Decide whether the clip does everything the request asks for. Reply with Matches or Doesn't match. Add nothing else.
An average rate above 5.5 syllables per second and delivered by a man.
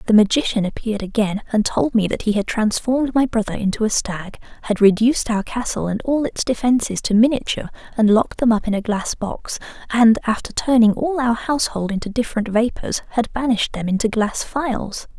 Doesn't match